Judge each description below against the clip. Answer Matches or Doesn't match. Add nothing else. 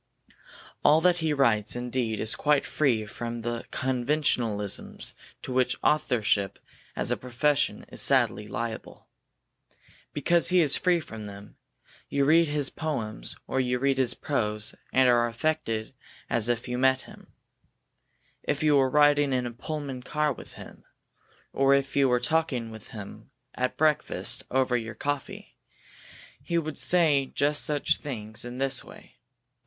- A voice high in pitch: Doesn't match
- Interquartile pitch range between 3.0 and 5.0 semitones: Matches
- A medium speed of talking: Matches